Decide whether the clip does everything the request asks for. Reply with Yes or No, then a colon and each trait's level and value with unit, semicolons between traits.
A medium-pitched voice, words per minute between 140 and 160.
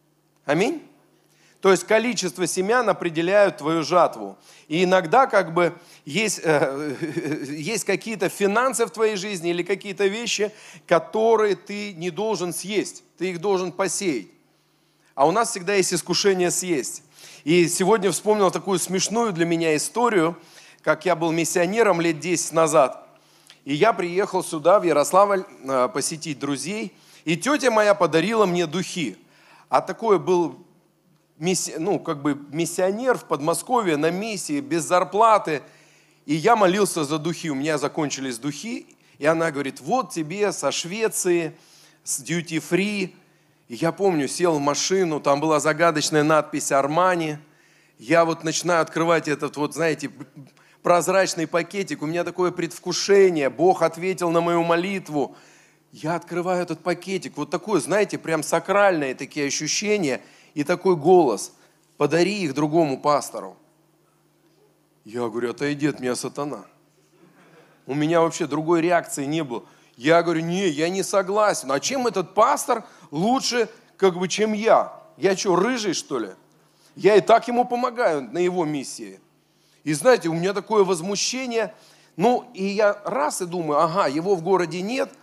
Yes: medium, 175 Hz; average, 145 wpm